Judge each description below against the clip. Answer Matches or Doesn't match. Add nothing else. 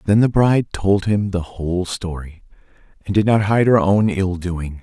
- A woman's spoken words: Doesn't match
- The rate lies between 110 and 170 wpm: Doesn't match